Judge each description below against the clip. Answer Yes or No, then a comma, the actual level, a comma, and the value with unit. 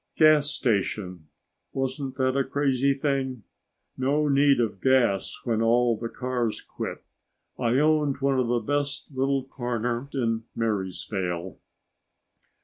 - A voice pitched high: No, low, 130 Hz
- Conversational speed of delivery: No, slow, 125 wpm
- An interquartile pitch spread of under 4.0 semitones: Yes, average, 3.2 semitones